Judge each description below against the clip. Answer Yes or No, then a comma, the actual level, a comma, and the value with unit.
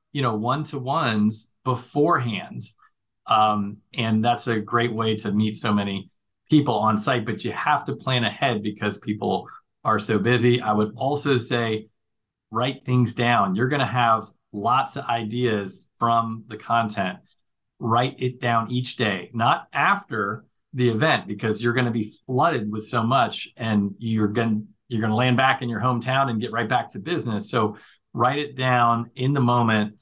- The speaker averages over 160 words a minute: Yes, average, 180 wpm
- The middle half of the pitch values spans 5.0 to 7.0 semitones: No, average, 2.8 semitones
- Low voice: Yes, low, 115 Hz